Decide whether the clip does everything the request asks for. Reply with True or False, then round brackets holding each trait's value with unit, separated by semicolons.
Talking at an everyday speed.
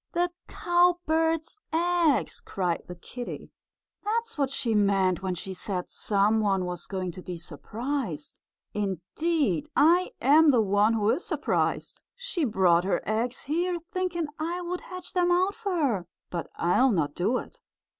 True (155 wpm)